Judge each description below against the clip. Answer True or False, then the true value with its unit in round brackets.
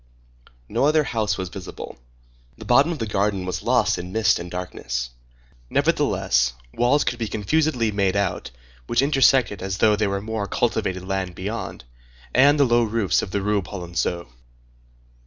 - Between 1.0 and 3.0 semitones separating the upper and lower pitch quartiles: False (4.2 semitones)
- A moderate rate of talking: True (160 wpm)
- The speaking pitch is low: True (105 Hz)